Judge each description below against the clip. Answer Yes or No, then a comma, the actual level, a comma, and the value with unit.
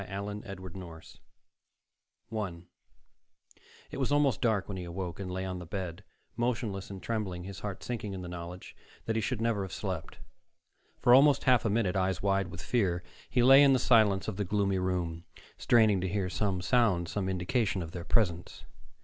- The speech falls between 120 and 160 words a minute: No, average, 185 wpm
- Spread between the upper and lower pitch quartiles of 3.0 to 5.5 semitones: Yes, average, 3.7 semitones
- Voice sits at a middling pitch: No, very low, 95 Hz